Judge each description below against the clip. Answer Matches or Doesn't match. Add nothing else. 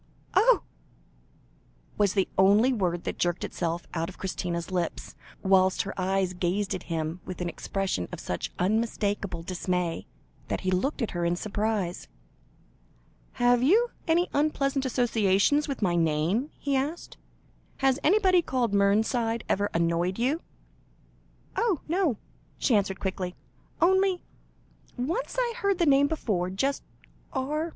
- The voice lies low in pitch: Doesn't match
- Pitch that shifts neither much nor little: Doesn't match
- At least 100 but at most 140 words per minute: Matches